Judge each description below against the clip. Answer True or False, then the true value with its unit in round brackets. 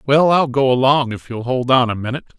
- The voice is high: False (130 Hz)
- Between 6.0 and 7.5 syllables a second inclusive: True (6.1 syllables/s)